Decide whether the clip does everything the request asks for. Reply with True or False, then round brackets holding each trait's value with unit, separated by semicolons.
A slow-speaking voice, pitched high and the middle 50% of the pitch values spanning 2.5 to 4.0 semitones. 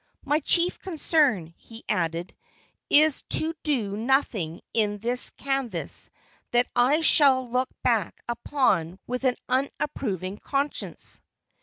False (115 wpm; 250 Hz; 5.4 semitones)